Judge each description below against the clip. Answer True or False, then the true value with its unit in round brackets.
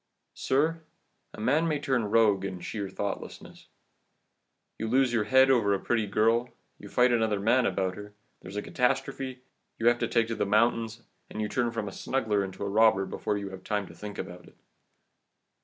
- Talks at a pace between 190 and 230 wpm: True (195 wpm)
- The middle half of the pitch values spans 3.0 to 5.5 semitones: True (3.4 semitones)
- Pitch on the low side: True (110 Hz)